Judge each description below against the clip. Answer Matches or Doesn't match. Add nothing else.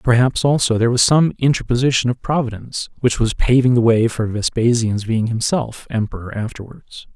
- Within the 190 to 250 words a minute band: Doesn't match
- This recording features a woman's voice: Doesn't match